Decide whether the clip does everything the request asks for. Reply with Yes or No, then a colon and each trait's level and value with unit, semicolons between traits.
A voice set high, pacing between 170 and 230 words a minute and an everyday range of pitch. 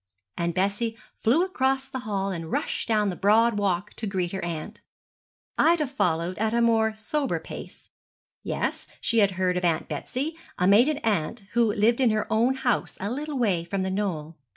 Yes: high, 210 Hz; average, 185 wpm; average, 4.4 semitones